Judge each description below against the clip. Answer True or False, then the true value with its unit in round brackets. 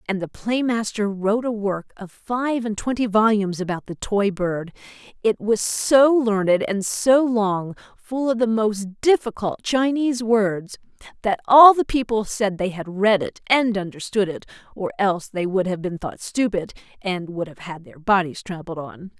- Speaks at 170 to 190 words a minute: True (180 wpm)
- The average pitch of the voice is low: False (205 Hz)